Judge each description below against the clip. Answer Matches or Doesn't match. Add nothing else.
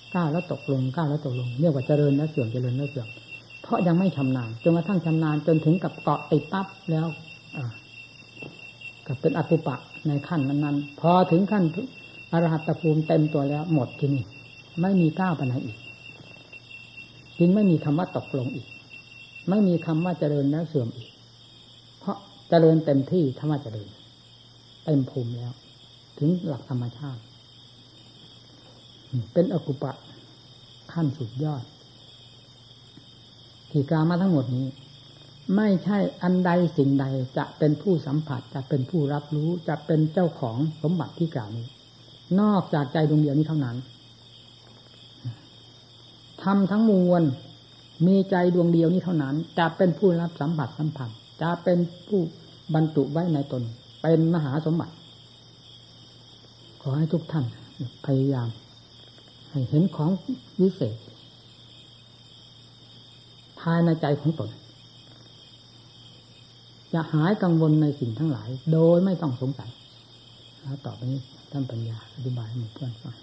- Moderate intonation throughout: Matches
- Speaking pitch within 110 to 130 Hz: Doesn't match